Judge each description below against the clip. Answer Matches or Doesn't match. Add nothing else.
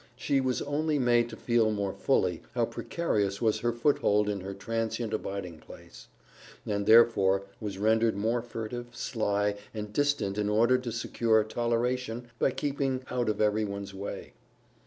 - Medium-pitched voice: Doesn't match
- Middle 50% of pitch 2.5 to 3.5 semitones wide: Matches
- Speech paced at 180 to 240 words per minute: Doesn't match